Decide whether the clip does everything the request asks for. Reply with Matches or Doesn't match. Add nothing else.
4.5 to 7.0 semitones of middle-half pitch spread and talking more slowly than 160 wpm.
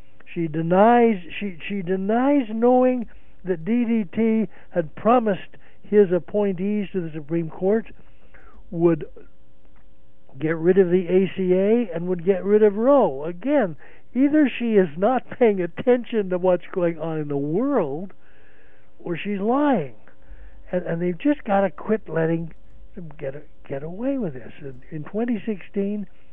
Matches